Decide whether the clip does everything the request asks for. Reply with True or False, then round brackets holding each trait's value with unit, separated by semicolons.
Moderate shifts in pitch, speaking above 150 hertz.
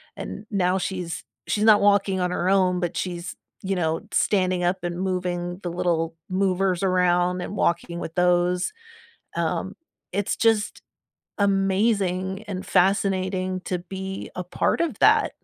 False (1.6 semitones; 185 Hz)